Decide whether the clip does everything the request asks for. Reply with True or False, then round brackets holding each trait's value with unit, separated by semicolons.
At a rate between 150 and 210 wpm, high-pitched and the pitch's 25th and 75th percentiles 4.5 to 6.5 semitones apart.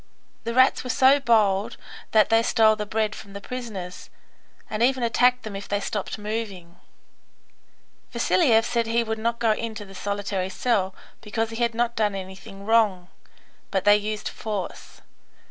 False (165 wpm; 220 Hz; 2.5 semitones)